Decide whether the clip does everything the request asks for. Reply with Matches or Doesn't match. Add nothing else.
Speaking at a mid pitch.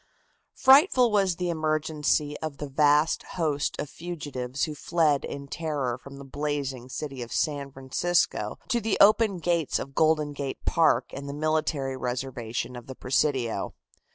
Matches